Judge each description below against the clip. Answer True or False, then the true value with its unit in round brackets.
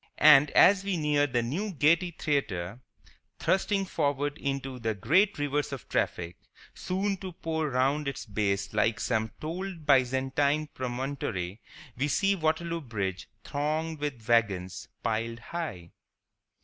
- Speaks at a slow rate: True (130 wpm)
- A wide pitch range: True (5.7 semitones)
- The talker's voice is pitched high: False (140 Hz)